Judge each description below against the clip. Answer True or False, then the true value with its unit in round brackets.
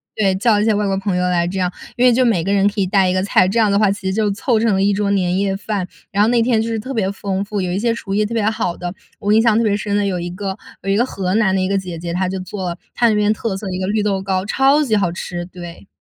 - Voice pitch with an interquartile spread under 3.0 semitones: True (2.4 semitones)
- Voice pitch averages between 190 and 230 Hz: True (200 Hz)